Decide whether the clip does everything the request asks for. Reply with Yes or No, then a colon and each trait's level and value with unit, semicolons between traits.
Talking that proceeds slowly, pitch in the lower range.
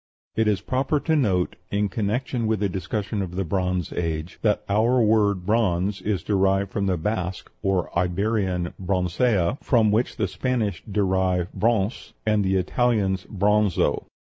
No: average, 150 wpm; low, 100 Hz